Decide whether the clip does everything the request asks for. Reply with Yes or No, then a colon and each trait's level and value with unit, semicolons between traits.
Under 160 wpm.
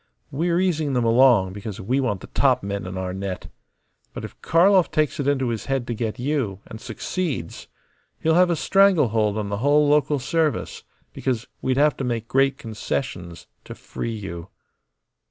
No: average, 180 wpm